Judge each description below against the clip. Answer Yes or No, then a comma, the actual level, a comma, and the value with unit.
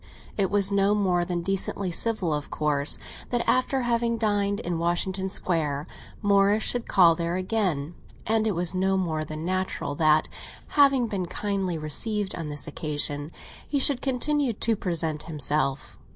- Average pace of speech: Yes, average, 155 wpm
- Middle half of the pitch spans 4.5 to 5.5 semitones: Yes, average, 5.0 semitones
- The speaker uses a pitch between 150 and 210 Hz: Yes, medium, 185 Hz